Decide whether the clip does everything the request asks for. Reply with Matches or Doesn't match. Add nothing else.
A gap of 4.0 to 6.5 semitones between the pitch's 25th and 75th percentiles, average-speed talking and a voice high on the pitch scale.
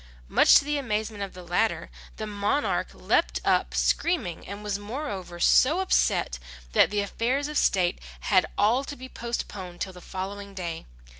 Matches